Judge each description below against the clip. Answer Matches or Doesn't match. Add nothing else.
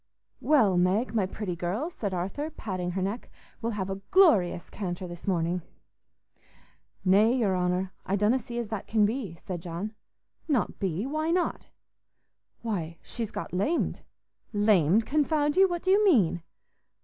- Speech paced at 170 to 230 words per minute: Doesn't match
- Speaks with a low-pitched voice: Doesn't match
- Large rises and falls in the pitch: Matches